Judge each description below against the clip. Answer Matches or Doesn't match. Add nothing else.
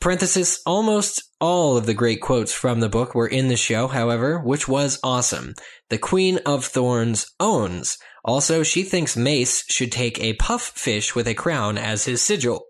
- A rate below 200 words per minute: Matches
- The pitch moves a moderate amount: Doesn't match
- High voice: Doesn't match